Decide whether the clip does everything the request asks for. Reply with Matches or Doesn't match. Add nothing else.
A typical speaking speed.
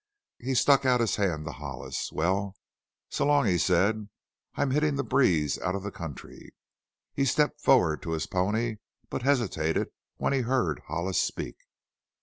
Matches